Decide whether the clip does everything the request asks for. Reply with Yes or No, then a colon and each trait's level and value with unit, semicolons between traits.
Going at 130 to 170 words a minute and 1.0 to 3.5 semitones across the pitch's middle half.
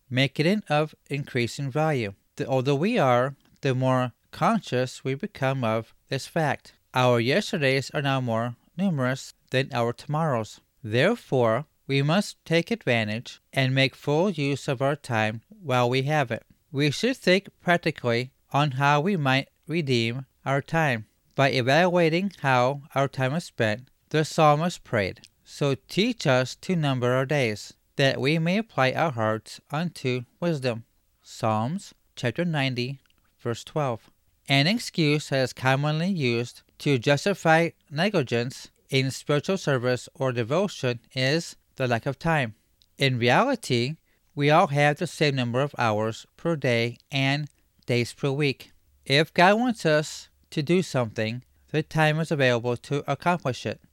No: average, 145 wpm; average, 4.3 semitones